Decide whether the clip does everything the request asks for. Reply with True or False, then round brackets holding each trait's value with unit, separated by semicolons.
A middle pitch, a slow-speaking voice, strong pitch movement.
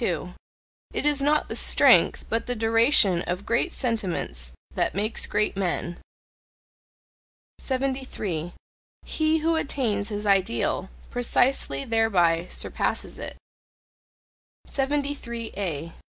False (220 Hz; 95 wpm; 6.6 semitones)